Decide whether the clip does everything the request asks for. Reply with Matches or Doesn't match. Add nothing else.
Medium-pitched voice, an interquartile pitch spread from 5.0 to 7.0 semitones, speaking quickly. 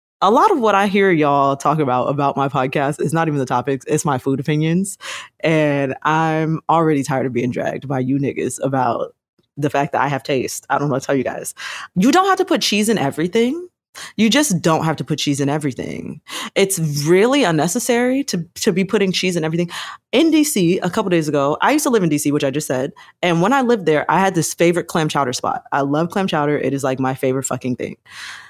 Matches